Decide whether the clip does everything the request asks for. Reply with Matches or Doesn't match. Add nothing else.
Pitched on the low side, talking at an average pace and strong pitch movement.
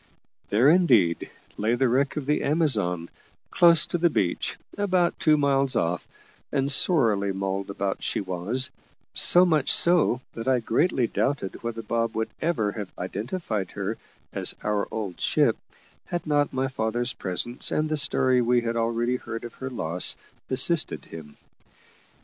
Matches